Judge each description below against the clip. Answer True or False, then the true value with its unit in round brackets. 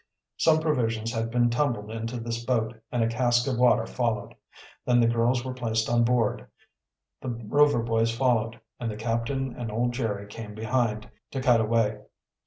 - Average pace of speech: True (175 wpm)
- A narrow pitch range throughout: True (1.6 semitones)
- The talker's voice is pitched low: True (115 Hz)